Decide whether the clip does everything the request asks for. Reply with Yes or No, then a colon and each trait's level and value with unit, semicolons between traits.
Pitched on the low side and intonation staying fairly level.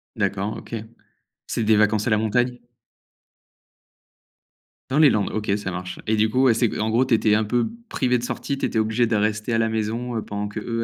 Yes: low, 110 Hz; narrow, 2.1 semitones